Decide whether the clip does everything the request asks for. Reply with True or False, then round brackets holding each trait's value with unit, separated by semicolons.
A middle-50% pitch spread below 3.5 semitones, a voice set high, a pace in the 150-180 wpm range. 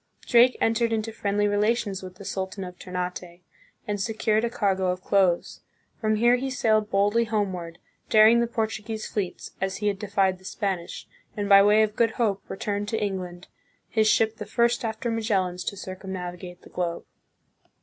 True (2.9 semitones; 205 Hz; 175 wpm)